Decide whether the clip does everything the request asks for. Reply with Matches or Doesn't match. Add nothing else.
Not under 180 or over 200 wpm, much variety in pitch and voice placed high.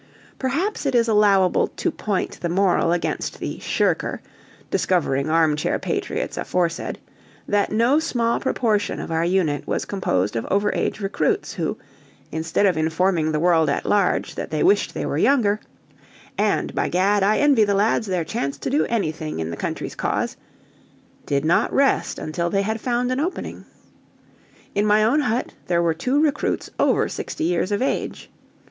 Doesn't match